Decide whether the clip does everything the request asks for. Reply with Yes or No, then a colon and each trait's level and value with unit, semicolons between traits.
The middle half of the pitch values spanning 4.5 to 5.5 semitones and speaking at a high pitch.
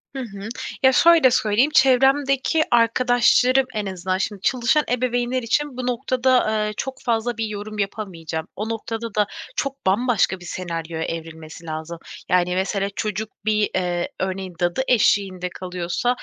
Yes: average, 5.2 semitones; high, 215 Hz